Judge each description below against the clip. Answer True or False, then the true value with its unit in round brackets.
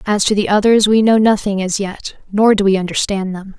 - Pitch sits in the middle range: False (205 Hz)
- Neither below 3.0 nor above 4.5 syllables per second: False (5.4 syllables/s)